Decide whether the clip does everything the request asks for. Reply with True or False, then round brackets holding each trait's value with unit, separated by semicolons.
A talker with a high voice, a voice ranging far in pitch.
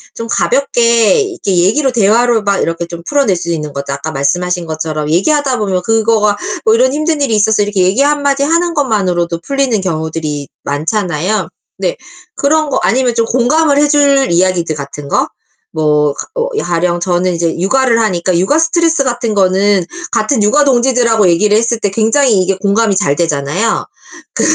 True (210 Hz; 7.3 semitones)